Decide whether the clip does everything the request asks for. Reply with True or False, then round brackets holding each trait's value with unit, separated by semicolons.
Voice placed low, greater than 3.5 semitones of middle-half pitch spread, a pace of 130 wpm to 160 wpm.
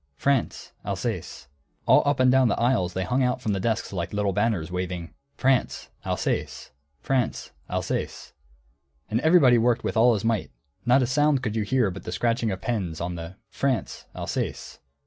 False (115 Hz; 5.2 semitones; 175 wpm)